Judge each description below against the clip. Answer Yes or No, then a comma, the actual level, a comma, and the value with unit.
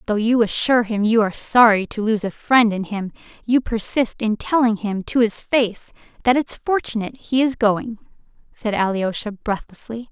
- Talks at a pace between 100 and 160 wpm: No, average, 180 wpm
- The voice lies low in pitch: No, high, 225 Hz